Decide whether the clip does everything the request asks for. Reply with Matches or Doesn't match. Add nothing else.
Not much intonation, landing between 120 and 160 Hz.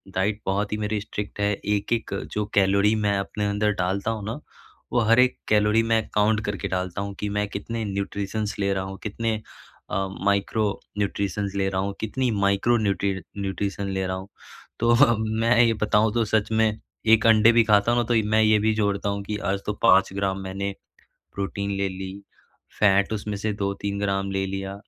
Doesn't match